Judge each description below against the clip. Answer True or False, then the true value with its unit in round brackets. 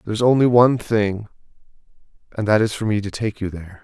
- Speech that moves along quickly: True (220 wpm)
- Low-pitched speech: True (105 Hz)